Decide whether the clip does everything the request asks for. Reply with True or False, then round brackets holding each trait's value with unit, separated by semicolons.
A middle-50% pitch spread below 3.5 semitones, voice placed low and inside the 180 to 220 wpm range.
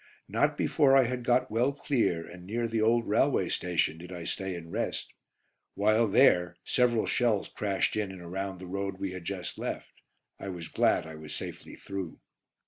False (4.7 semitones; 100 Hz; 185 wpm)